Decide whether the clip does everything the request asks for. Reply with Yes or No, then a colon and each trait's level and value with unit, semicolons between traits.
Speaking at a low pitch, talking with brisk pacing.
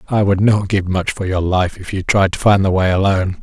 Yes: very low, 95 Hz; fast, 280 wpm